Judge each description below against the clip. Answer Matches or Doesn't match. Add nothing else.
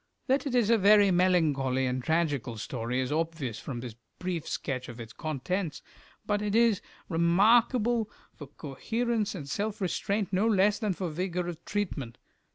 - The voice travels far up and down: Matches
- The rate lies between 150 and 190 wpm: Matches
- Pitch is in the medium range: Matches